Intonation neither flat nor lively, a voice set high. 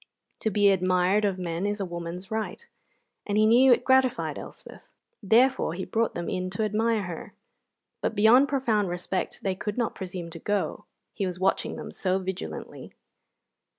Yes: average, 3.3 semitones; high, 200 Hz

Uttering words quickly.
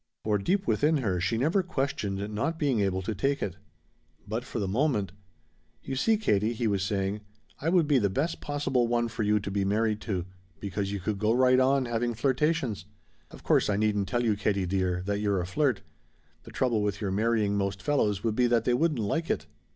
Yes: fast, 215 wpm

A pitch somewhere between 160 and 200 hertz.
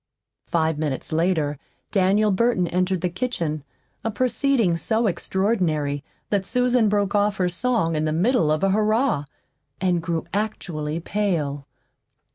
Yes: medium, 185 Hz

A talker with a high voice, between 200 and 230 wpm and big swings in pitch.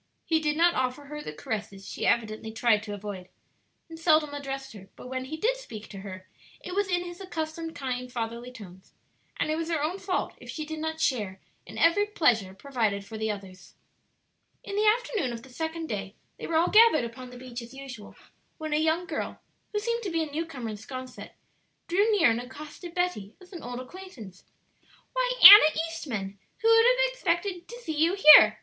Yes: very high, 300 Hz; fast, 205 wpm; wide, 7.2 semitones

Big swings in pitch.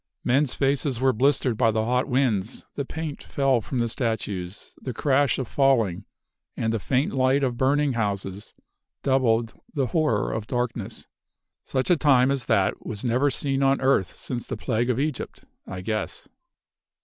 No: average, 3.6 semitones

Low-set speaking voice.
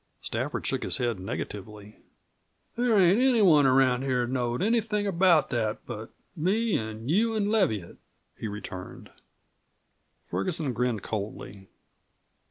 Yes: low, 130 Hz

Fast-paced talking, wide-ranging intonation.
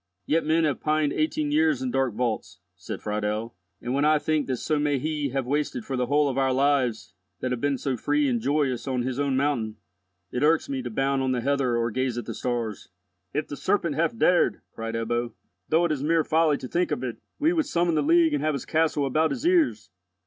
No: fast, 235 wpm; average, 3.9 semitones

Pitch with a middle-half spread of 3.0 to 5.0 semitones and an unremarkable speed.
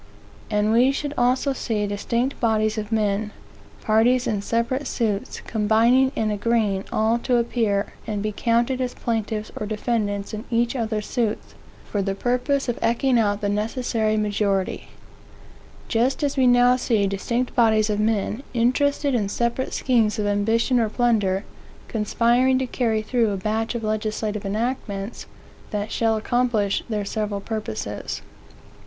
No: narrow, 2.5 semitones; average, 150 wpm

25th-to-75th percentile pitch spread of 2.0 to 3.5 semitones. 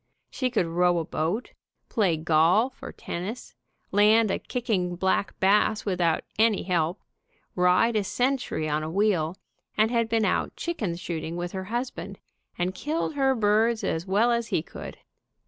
No: average, 4.6 semitones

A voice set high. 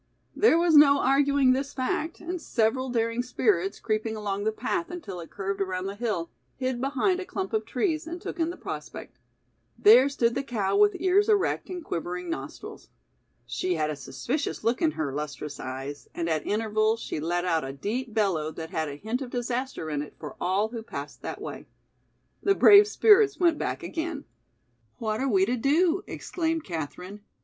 Yes: high, 230 Hz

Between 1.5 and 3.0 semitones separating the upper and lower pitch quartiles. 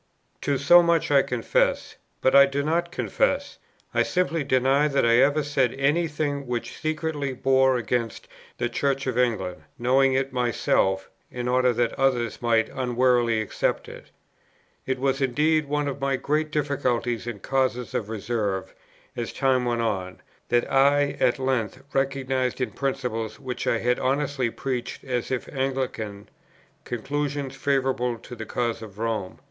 Yes: average, 2.7 semitones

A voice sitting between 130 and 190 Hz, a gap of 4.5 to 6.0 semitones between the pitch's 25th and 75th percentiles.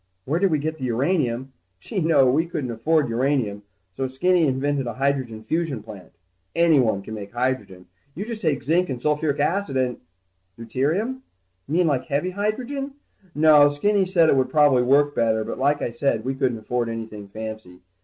Yes: medium, 140 Hz; average, 5.2 semitones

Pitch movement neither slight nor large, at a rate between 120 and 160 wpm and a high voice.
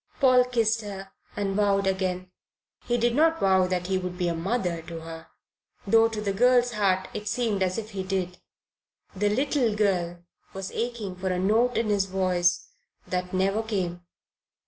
No: average, 3.6 semitones; average, 175 wpm; high, 195 Hz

